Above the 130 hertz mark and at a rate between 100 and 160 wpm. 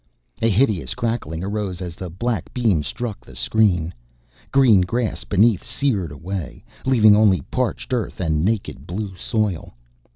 No: low, 100 Hz; average, 140 wpm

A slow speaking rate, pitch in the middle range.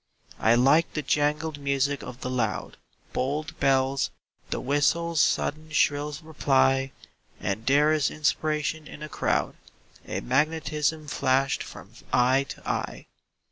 Yes: slow, 130 wpm; medium, 145 Hz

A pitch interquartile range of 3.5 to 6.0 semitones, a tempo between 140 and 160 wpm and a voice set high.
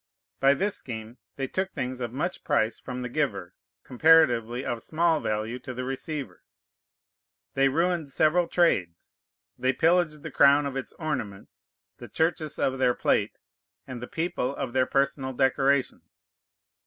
No: average, 4.1 semitones; average, 150 wpm; low, 135 Hz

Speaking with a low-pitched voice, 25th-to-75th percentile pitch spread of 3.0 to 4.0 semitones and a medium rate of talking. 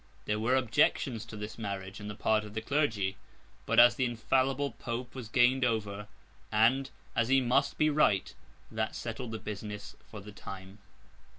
Yes: low, 115 Hz; average, 3.6 semitones; average, 175 wpm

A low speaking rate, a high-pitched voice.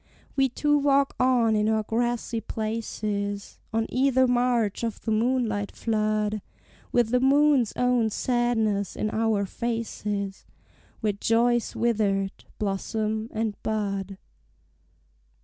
Yes: slow, 115 wpm; high, 225 Hz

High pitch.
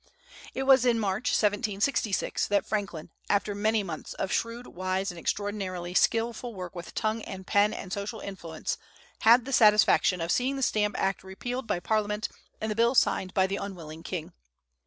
Yes: high, 205 Hz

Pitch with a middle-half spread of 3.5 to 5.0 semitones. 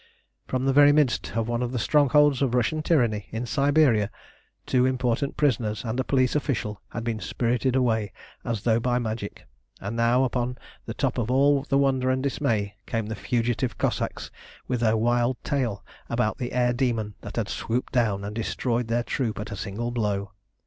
No: average, 2.8 semitones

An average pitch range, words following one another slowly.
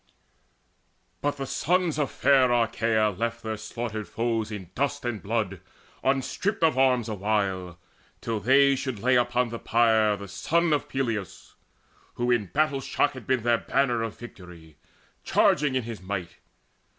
No: average, 4.0 semitones; average, 150 wpm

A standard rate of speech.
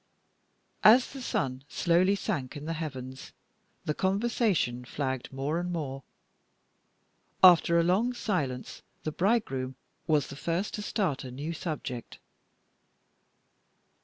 No: slow, 120 wpm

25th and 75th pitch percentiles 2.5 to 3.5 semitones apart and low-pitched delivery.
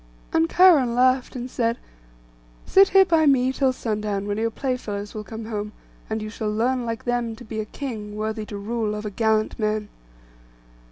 No: average, 3.1 semitones; high, 225 Hz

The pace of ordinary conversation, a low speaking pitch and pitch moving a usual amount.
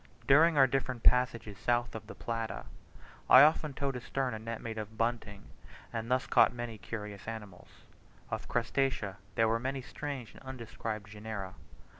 Yes: average, 160 wpm; low, 115 Hz; average, 3.1 semitones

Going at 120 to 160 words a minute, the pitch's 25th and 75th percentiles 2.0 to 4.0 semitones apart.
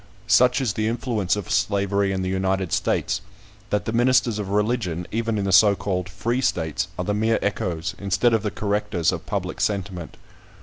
No: average, 185 wpm; average, 2.8 semitones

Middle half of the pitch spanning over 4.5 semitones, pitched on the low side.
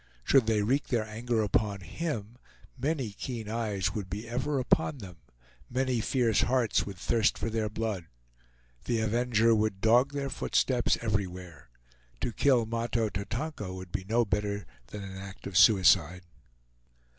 No: average, 3.5 semitones; low, 110 Hz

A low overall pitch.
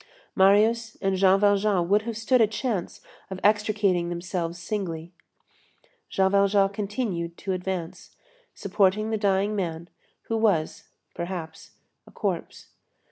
No: high, 195 Hz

